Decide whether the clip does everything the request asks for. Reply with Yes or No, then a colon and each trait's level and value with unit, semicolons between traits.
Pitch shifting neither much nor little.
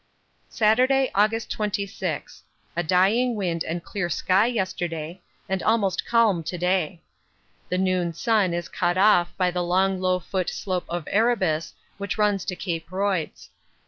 Yes: average, 3.1 semitones